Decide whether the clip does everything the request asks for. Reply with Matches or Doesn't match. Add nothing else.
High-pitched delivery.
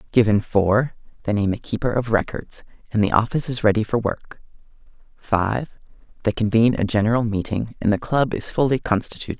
Doesn't match